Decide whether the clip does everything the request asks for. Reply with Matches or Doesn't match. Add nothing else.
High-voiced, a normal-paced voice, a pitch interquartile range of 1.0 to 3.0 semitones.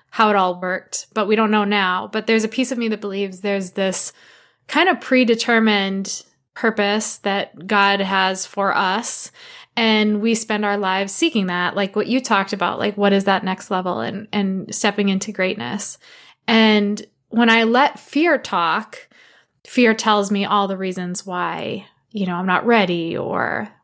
Matches